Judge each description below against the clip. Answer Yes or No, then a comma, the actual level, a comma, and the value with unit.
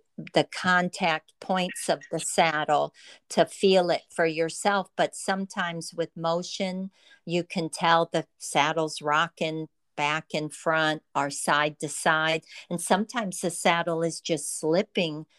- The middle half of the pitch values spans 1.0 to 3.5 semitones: Yes, narrow, 2.6 semitones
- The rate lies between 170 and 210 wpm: No, slow, 135 wpm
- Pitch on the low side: No, medium, 165 Hz